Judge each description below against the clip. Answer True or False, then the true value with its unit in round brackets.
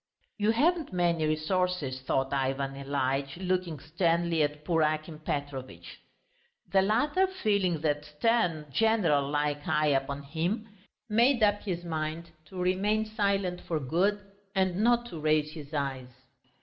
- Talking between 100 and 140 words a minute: True (135 wpm)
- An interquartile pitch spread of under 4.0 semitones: False (5.3 semitones)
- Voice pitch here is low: False (165 Hz)